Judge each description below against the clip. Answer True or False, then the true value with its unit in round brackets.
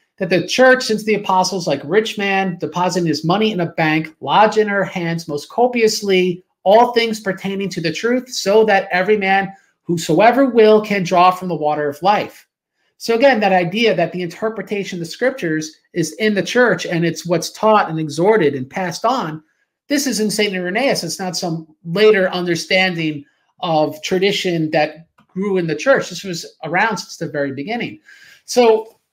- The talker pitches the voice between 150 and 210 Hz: True (190 Hz)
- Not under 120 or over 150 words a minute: False (180 wpm)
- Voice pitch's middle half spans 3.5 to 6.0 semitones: True (4.4 semitones)